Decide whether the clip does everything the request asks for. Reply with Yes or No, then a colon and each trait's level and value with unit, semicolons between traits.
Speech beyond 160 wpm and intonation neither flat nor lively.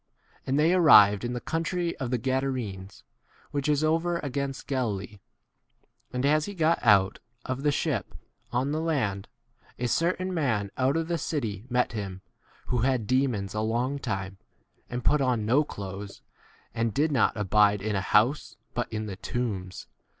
No: average, 180 wpm; wide, 5.7 semitones